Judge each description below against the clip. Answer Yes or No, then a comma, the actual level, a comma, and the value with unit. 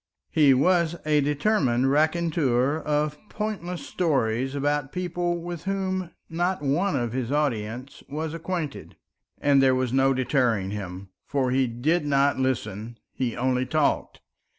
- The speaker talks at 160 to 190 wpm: No, slow, 135 wpm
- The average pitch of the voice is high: No, medium, 145 Hz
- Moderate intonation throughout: Yes, average, 4.5 semitones